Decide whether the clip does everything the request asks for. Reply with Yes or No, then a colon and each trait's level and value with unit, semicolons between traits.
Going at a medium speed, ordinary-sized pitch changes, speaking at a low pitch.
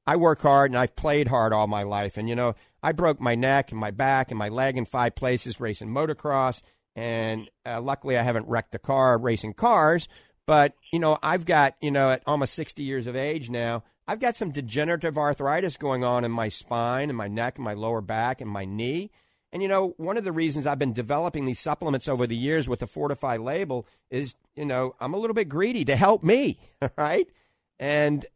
No: fast, 220 wpm; average, 4.1 semitones; low, 130 Hz